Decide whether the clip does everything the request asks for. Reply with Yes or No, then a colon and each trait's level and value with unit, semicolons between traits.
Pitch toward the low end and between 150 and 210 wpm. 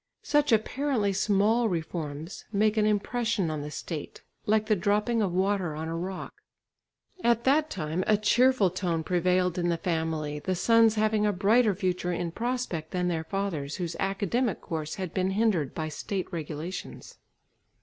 No: high, 190 Hz; average, 160 wpm